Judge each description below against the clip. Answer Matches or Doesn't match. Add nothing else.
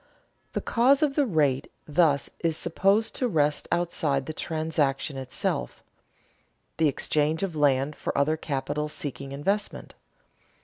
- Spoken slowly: Matches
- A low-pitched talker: Doesn't match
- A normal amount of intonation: Matches